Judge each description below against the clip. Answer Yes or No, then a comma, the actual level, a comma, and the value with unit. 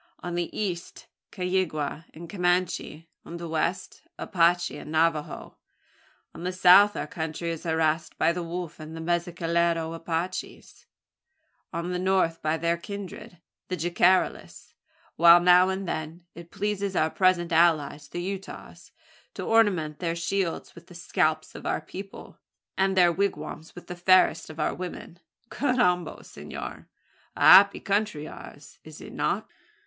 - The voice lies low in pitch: No, medium, 175 Hz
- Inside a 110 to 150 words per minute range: Yes, average, 145 wpm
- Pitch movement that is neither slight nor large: No, narrow, 2.1 semitones